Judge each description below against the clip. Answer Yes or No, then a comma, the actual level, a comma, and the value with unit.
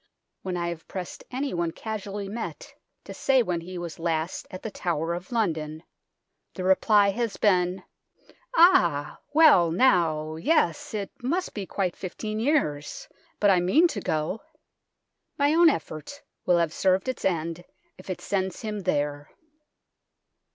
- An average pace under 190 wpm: Yes, average, 150 wpm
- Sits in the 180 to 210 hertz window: Yes, medium, 185 Hz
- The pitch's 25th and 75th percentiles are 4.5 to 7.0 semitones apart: Yes, average, 5.0 semitones